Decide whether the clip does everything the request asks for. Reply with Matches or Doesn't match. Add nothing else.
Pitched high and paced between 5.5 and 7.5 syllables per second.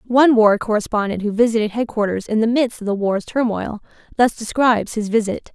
Matches